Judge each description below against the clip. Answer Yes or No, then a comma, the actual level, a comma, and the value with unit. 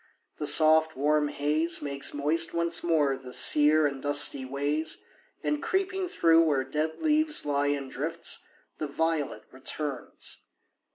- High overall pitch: No, medium, 150 Hz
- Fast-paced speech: No, slow, 135 wpm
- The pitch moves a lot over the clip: No, narrow, 2.5 semitones